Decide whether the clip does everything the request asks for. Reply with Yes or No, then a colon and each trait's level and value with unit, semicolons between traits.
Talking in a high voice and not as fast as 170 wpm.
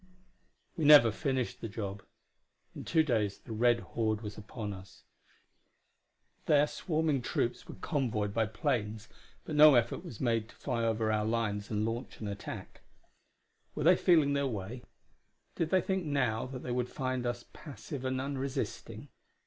No: low, 120 Hz; average, 160 wpm